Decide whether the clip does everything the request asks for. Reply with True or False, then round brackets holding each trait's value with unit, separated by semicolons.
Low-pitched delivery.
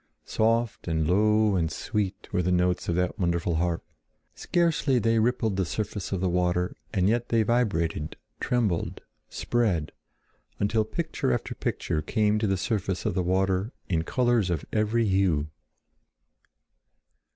True (95 Hz)